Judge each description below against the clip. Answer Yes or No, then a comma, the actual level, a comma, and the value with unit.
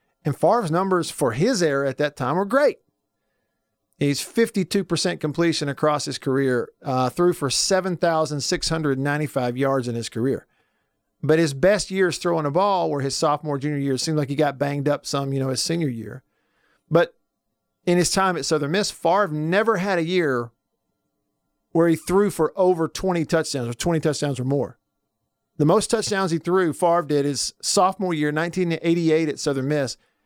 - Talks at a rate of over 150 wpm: Yes, average, 175 wpm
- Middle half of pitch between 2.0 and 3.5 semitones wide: No, average, 4.2 semitones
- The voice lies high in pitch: No, medium, 155 Hz